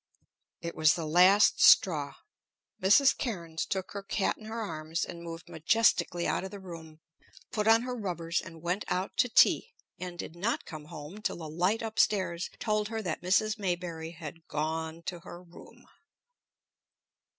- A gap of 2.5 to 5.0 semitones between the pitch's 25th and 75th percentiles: Yes, average, 3.9 semitones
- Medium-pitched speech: Yes, medium, 175 Hz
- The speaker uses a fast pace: No, average, 170 wpm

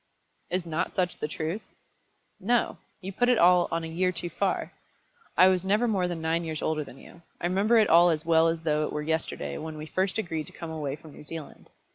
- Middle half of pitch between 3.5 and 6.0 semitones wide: No, average, 2.7 semitones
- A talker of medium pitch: Yes, medium, 165 Hz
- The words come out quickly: Yes, fast, 230 wpm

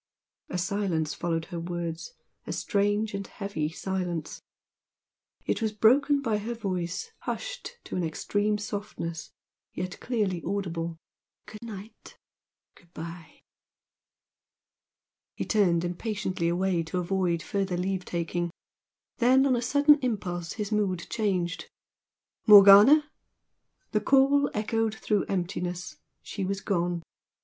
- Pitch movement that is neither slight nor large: Yes, average, 3.8 semitones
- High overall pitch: Yes, high, 195 Hz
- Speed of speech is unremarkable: No, slow, 120 wpm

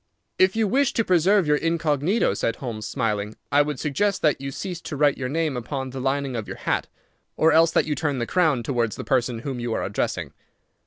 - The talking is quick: Yes, fast, 220 wpm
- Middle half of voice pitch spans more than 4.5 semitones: Yes, average, 4.9 semitones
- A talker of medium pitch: Yes, medium, 145 Hz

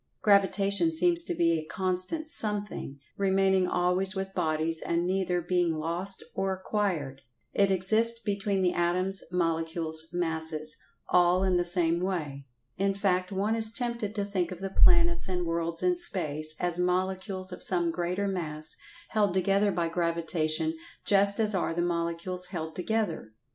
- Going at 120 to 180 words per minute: Yes, average, 150 wpm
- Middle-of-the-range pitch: Yes, medium, 180 Hz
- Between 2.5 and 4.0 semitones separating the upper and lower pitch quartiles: Yes, average, 2.9 semitones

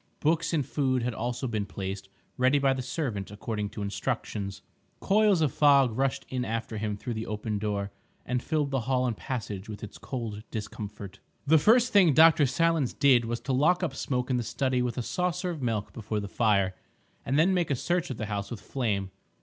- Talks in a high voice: No, low, 125 Hz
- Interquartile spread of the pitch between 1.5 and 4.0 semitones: No, average, 5.3 semitones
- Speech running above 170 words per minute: Yes, fast, 205 wpm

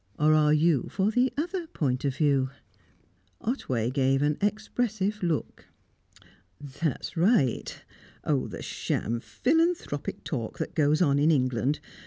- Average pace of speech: No, slow, 130 wpm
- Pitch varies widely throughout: Yes, wide, 7.5 semitones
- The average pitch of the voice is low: No, medium, 150 Hz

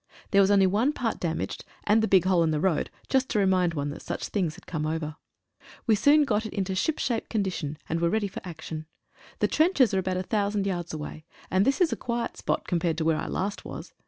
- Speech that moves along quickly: Yes, fast, 240 wpm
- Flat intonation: No, average, 4.7 semitones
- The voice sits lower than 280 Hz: Yes, high, 190 Hz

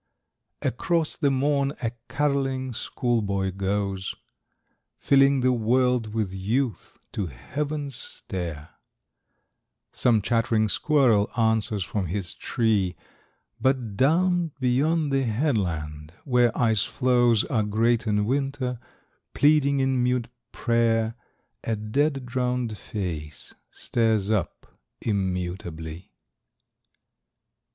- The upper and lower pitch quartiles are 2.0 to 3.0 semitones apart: No, average, 4.8 semitones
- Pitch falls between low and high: No, low, 115 Hz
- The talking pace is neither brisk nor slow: No, slow, 100 wpm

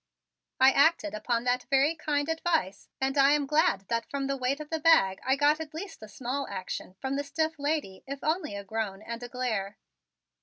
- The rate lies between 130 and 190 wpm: No, fast, 205 wpm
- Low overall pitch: No, very high, 275 Hz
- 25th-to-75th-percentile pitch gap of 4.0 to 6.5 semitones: Yes, average, 4.8 semitones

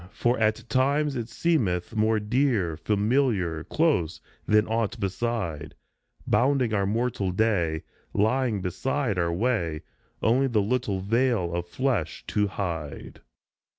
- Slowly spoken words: Yes, slow, 120 wpm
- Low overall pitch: Yes, low, 110 Hz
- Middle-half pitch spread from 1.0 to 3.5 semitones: No, wide, 5.5 semitones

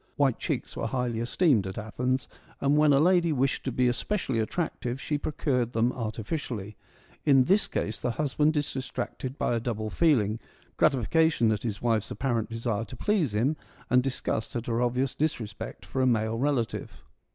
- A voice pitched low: Yes, low, 125 Hz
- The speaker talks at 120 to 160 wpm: No, average, 180 wpm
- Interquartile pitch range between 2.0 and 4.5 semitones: Yes, average, 4.1 semitones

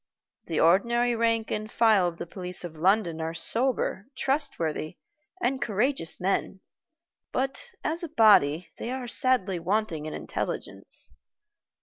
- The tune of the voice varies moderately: No, wide, 6.0 semitones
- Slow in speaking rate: Yes, slow, 130 wpm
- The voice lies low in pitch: No, high, 210 Hz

